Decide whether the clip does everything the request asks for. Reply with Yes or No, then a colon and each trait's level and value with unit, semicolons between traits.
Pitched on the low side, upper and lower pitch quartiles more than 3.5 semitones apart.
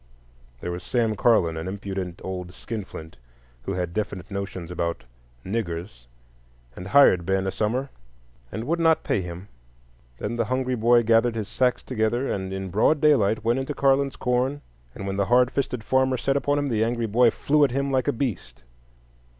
Yes: low, 110 Hz; average, 5.2 semitones